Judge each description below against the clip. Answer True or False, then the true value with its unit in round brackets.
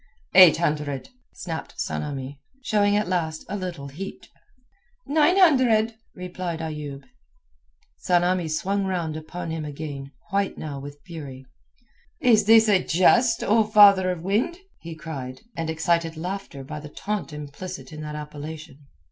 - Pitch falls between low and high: True (170 Hz)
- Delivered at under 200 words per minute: True (140 wpm)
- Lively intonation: False (4.7 semitones)